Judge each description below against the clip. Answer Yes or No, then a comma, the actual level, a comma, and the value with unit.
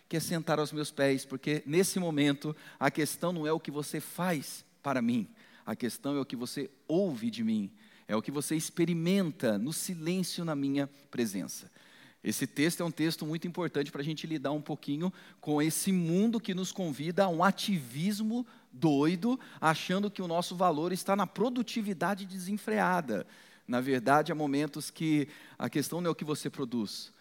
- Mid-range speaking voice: Yes, medium, 165 Hz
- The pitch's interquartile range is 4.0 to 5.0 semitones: Yes, average, 4.5 semitones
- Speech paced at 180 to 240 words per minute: Yes, fast, 185 wpm